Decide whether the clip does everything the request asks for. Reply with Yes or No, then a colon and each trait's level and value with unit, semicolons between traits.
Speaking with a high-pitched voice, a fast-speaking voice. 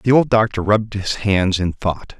No: low, 100 Hz; fast, 220 wpm